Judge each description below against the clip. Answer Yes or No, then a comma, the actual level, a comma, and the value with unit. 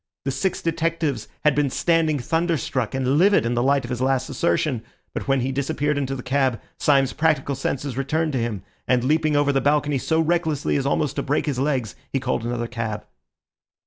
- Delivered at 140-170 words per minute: No, average, 200 wpm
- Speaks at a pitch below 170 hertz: Yes, medium, 140 Hz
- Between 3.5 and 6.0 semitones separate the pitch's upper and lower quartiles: No, average, 3.1 semitones